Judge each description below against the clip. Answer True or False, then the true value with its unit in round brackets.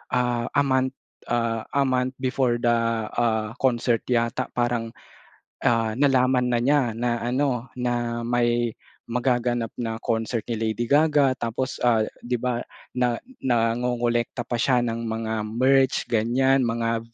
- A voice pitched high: False (120 Hz)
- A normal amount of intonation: False (1.6 semitones)